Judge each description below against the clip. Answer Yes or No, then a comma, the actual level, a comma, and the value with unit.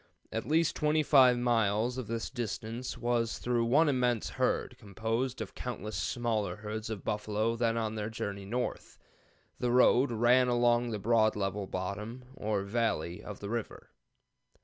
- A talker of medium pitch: No, low, 115 Hz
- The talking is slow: No, average, 150 wpm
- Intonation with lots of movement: No, narrow, 2.6 semitones